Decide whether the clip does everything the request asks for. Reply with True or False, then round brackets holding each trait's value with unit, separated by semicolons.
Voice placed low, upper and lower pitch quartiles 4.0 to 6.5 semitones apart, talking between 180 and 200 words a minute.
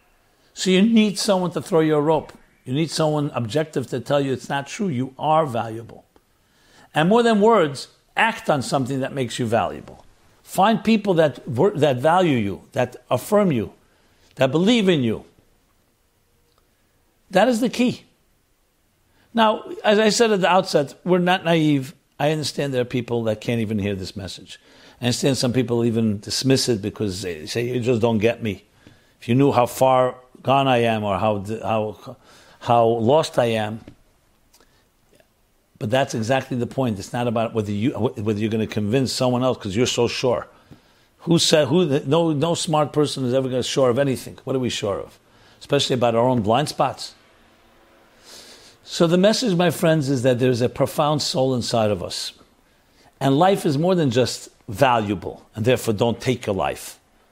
True (130 Hz; 5.4 semitones; 185 wpm)